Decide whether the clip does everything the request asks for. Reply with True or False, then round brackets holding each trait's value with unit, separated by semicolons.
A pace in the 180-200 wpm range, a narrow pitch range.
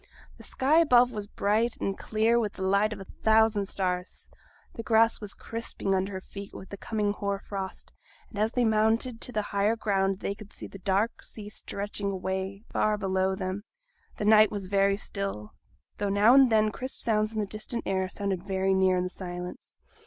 True (195 wpm; 2.2 semitones)